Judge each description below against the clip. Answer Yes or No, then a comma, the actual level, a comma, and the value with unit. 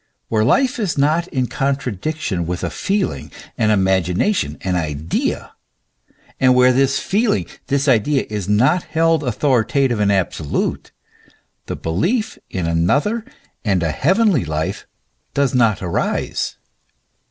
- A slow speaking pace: Yes, slow, 130 wpm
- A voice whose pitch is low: Yes, low, 125 Hz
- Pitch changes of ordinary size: No, wide, 8.6 semitones